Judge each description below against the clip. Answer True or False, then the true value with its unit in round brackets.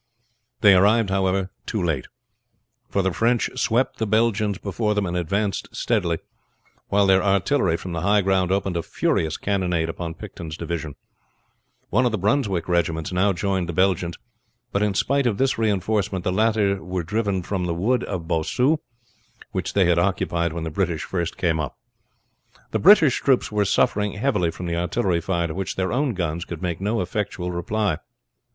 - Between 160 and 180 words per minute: True (175 wpm)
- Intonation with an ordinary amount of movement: True (3.4 semitones)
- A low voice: True (95 Hz)